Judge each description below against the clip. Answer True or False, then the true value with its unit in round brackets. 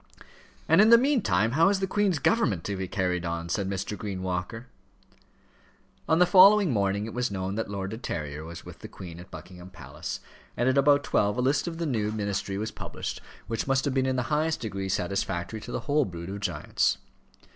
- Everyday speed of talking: False (210 wpm)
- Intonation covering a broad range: True (7.3 semitones)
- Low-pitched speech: True (105 Hz)